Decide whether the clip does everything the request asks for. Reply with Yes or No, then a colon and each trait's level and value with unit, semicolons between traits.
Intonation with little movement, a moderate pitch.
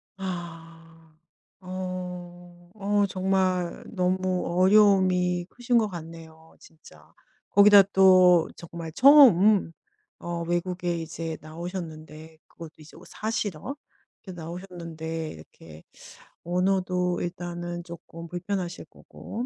Yes: narrow, 2.1 semitones; medium, 175 Hz